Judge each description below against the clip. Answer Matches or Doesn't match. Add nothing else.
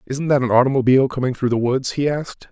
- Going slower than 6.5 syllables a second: Doesn't match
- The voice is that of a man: Matches